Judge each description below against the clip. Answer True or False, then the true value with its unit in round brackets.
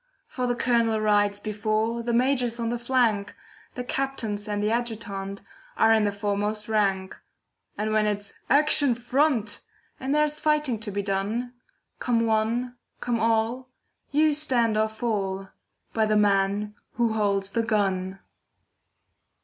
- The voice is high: True (220 Hz)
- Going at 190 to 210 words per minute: False (140 wpm)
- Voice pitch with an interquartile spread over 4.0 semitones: False (2.9 semitones)